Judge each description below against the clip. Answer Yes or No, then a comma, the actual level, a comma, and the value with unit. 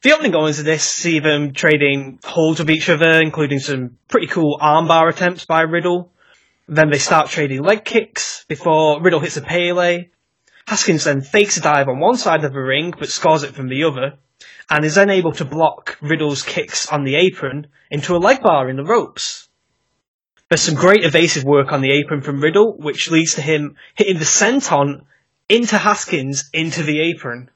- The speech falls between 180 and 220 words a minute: Yes, average, 190 wpm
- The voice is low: No, medium, 160 Hz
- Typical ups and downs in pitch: Yes, average, 3.2 semitones